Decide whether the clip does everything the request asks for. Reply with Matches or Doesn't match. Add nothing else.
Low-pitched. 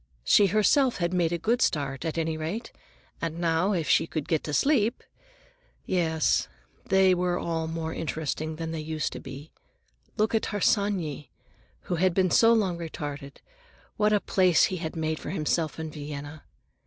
Doesn't match